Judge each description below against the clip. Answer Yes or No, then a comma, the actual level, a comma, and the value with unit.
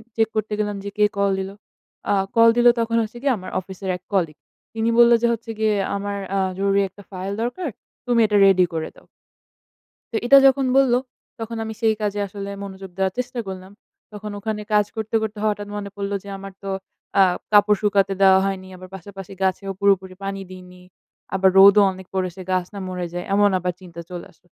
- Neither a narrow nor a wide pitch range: No, narrow, 2.3 semitones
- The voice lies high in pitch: Yes, high, 200 Hz